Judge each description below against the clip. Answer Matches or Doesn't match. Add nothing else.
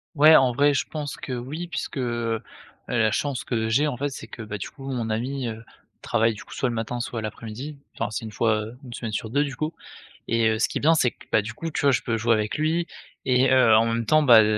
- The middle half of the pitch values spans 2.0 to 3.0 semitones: Doesn't match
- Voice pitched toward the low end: Matches